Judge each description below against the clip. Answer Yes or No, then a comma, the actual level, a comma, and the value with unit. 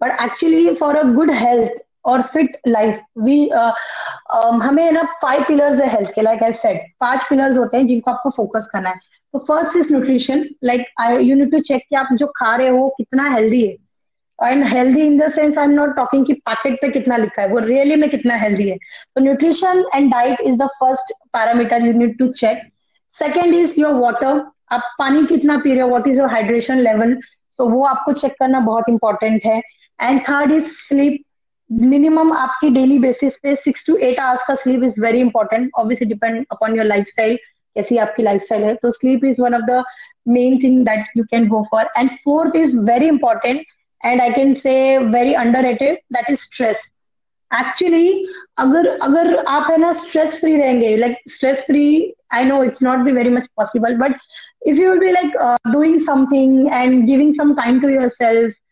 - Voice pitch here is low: No, very high, 260 Hz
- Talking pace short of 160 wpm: No, average, 200 wpm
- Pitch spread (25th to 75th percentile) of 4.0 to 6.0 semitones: No, average, 3.5 semitones